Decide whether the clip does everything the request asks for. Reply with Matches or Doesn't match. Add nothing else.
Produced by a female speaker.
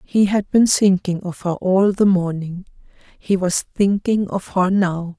Matches